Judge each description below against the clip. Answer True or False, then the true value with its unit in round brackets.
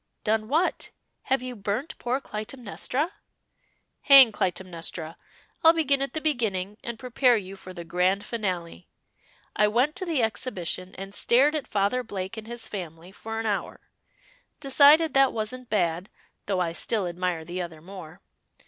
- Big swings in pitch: True (5.7 semitones)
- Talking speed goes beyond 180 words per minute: False (155 wpm)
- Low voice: False (215 Hz)